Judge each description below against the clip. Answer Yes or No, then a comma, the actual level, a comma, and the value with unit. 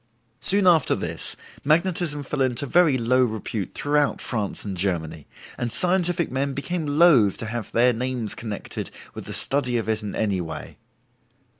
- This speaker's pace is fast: No, average, 160 wpm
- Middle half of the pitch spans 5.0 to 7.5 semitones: Yes, wide, 5.6 semitones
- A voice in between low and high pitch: No, low, 125 Hz